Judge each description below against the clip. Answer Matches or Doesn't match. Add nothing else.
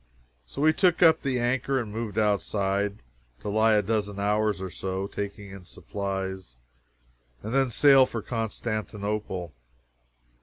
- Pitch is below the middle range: Matches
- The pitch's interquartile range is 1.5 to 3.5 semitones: Matches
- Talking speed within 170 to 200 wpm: Doesn't match